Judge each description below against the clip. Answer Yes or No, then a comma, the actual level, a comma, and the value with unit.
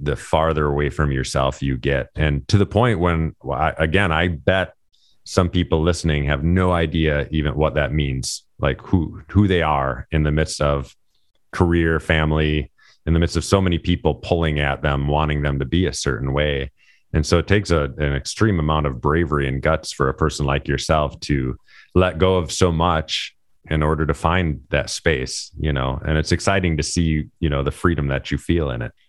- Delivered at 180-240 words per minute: Yes, average, 200 wpm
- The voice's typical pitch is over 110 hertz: No, very low, 75 Hz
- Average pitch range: Yes, average, 3.1 semitones